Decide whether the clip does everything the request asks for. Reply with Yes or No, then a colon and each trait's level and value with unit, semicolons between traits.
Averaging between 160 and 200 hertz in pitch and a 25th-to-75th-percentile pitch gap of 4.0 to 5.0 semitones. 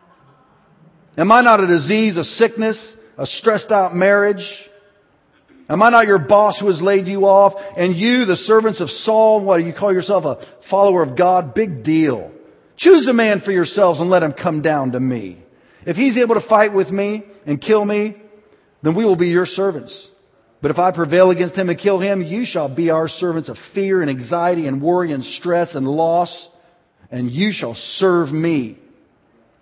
No: medium, 185 Hz; average, 3.4 semitones